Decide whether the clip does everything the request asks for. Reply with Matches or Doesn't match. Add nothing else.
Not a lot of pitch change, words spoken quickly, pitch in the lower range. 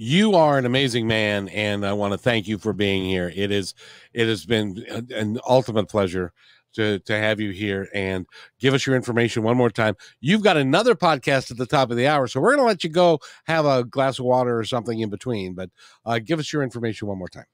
Doesn't match